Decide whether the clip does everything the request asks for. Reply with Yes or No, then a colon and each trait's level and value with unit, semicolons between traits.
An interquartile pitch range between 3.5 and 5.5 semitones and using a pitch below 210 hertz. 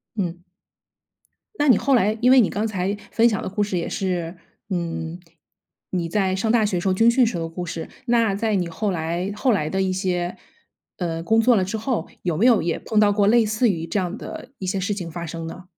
Yes: average, 4.0 semitones; high, 190 Hz